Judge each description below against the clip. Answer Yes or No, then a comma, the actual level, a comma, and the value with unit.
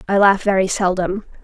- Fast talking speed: No, average, 170 wpm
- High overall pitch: Yes, high, 195 Hz